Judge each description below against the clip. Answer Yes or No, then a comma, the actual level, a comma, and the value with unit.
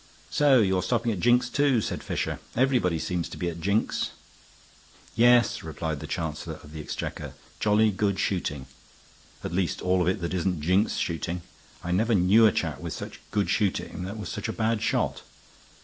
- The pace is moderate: Yes, average, 180 wpm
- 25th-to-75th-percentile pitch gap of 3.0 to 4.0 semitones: No, average, 4.6 semitones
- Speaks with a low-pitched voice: Yes, very low, 95 Hz